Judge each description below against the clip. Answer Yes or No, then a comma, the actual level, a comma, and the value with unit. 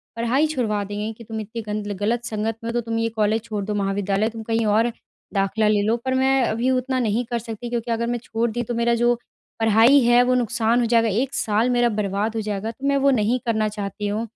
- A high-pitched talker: Yes, high, 225 Hz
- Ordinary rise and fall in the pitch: No, narrow, 2.2 semitones